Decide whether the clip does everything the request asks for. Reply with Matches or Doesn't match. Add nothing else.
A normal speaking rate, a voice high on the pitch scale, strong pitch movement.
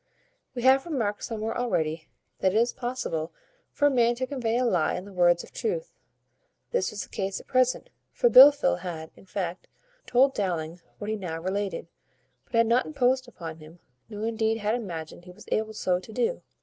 Matches